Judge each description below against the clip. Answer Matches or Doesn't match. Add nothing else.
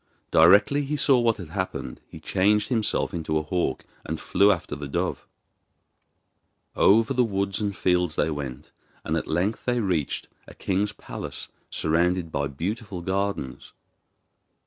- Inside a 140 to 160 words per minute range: Matches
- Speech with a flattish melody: Doesn't match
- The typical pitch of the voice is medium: Doesn't match